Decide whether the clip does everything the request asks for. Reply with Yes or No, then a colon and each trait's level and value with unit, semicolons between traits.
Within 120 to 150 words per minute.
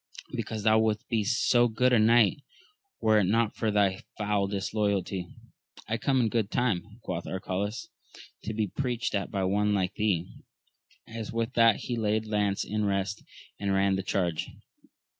No: average, 170 wpm